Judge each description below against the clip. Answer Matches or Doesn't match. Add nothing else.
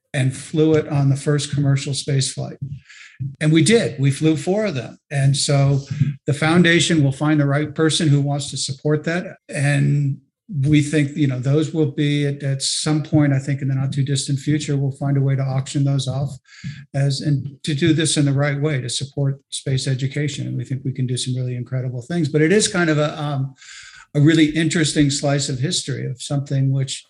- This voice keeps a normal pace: Doesn't match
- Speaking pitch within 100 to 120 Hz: Doesn't match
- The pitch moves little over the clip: Matches